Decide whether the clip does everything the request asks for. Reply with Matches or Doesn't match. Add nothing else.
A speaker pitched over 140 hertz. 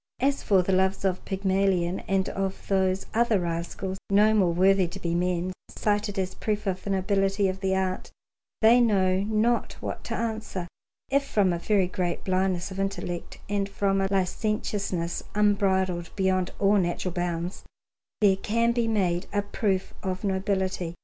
Matches